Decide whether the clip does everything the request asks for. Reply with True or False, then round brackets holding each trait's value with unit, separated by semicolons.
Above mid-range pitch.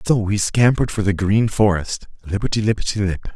False (100 Hz)